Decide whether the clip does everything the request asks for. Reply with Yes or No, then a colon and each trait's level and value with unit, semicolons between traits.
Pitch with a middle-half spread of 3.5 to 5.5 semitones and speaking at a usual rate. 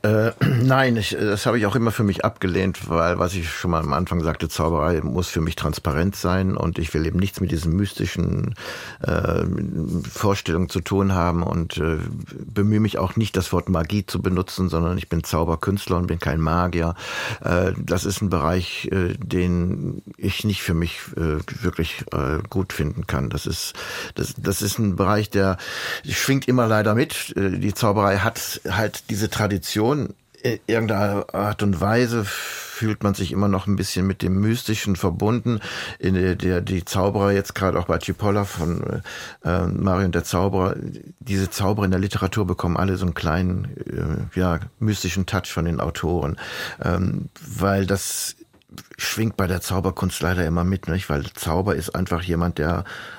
No: average, 2.8 semitones; average, 180 wpm